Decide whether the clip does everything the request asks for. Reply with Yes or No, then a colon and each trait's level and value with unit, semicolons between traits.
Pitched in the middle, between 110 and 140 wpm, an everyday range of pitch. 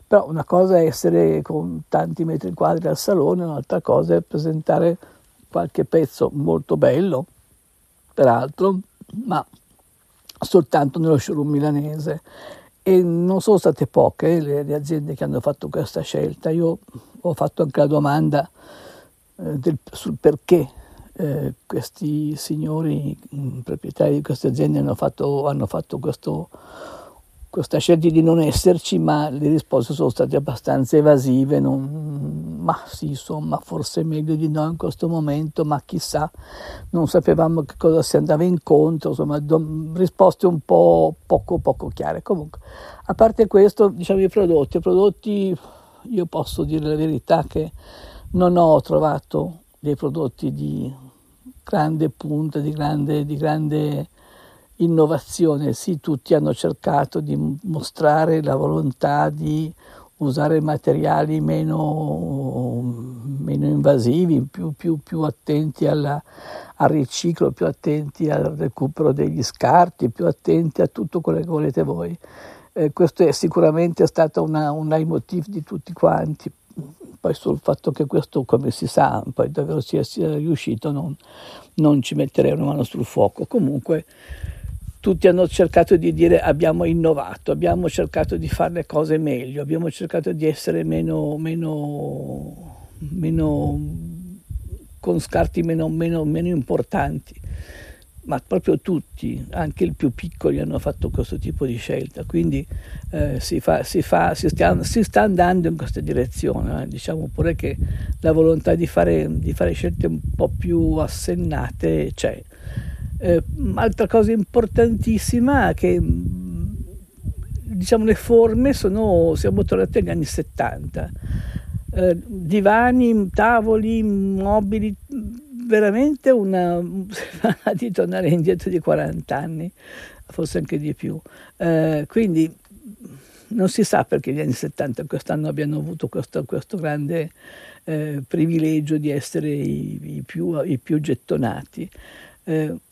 Yes: medium, 155 Hz; average, 135 wpm; average, 3.8 semitones